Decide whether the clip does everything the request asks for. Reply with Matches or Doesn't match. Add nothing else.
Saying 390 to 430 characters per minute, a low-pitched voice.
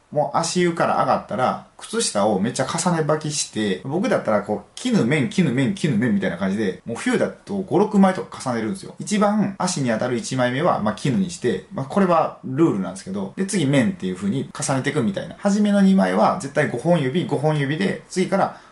Doesn't match